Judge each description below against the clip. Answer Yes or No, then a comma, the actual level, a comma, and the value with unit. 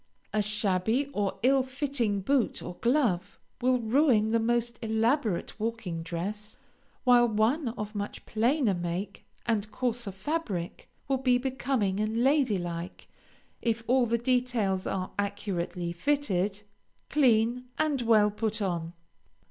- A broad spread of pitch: No, average, 4.0 semitones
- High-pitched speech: Yes, high, 220 Hz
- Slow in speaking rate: Yes, slow, 130 wpm